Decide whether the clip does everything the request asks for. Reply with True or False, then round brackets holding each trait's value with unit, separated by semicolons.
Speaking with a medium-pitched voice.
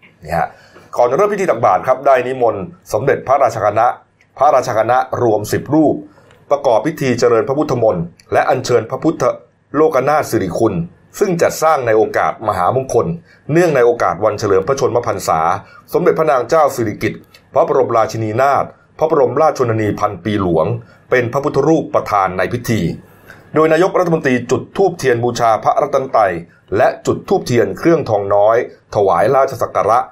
False (120 Hz)